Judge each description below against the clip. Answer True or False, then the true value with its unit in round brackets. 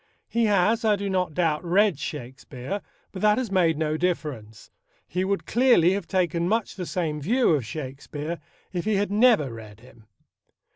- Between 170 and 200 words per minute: True (175 wpm)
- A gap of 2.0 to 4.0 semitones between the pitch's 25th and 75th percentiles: False (5.3 semitones)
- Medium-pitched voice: True (175 Hz)